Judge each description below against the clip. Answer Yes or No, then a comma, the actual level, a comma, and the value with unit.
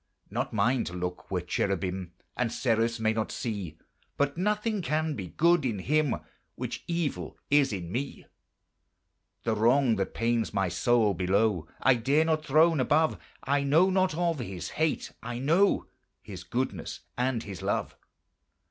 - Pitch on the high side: No, low, 120 Hz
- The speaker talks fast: No, average, 155 wpm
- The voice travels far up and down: Yes, wide, 7.4 semitones